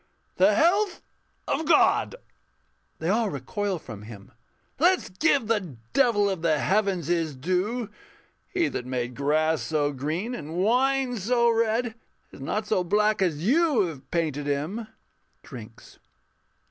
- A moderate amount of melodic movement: No, wide, 7.3 semitones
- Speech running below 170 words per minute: Yes, average, 140 wpm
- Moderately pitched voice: No, high, 195 Hz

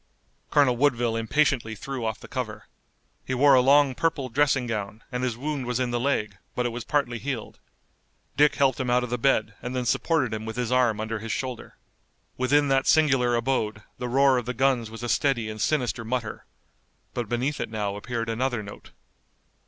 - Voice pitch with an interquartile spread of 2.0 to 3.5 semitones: Yes, average, 2.9 semitones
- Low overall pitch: Yes, low, 125 Hz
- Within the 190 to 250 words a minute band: Yes, average, 200 wpm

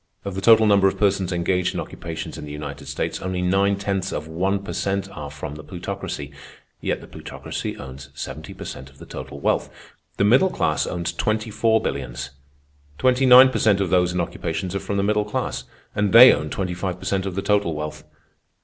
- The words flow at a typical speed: No, fast, 215 wpm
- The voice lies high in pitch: No, very low, 95 Hz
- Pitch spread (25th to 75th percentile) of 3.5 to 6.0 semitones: Yes, average, 4.3 semitones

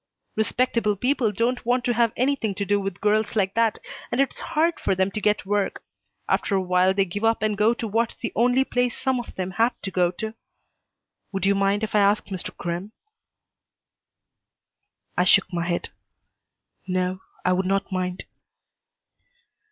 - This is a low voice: No, high, 205 Hz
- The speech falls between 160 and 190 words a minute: Yes, average, 175 wpm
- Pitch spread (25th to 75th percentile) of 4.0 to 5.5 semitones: No, average, 3.6 semitones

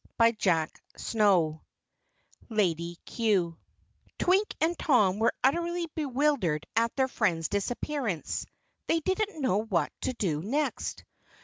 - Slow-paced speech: Yes, slow, 110 wpm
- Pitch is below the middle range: No, high, 225 Hz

